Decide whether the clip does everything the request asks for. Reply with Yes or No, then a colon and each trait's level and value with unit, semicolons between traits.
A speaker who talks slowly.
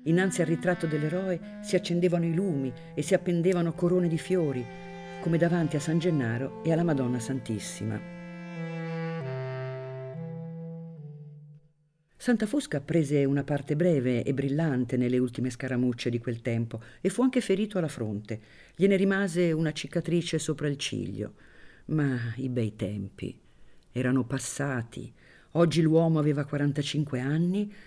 No: average, 130 wpm